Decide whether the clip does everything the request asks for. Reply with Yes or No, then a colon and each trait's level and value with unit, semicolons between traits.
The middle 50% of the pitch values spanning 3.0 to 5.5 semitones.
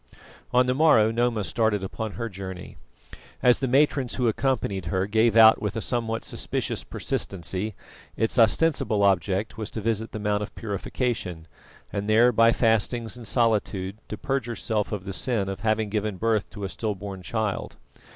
No: narrow, 2.6 semitones